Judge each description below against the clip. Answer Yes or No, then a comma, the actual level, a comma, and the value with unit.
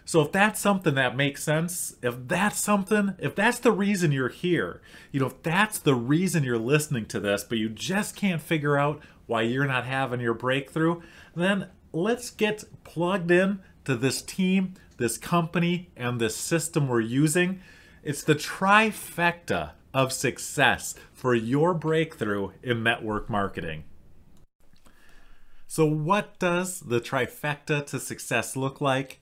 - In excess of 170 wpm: No, average, 150 wpm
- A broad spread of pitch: Yes, wide, 6.2 semitones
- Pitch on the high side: No, medium, 150 Hz